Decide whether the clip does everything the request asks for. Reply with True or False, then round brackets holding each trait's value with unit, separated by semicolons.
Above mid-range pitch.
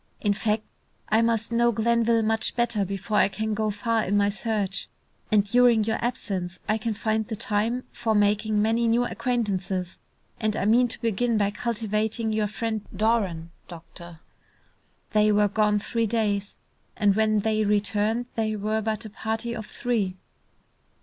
True (215 Hz)